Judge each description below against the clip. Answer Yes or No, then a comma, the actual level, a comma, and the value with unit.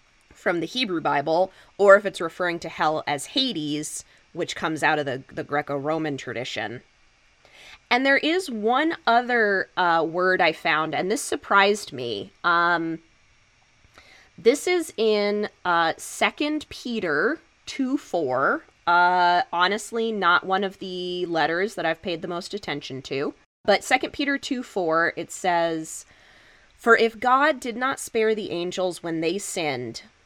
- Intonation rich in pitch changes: Yes, wide, 6.1 semitones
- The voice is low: No, medium, 180 Hz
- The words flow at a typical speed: Yes, average, 145 wpm